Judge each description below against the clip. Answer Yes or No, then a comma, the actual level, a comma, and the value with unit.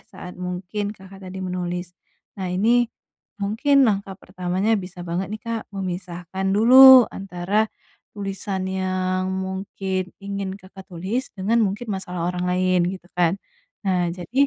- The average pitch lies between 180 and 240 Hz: Yes, high, 190 Hz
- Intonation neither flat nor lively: No, narrow, 2.3 semitones